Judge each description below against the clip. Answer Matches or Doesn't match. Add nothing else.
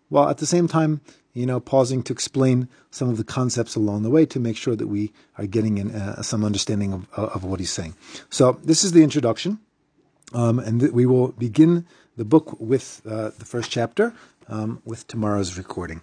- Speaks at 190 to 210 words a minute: Matches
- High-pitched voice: Doesn't match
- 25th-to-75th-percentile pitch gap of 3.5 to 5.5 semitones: Matches